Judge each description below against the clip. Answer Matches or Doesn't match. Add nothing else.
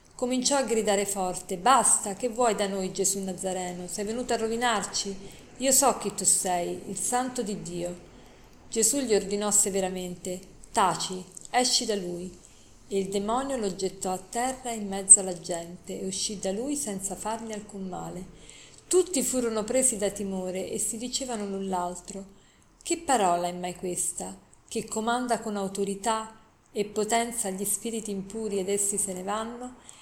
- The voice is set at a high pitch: Matches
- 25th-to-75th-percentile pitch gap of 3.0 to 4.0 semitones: Matches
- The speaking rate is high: Doesn't match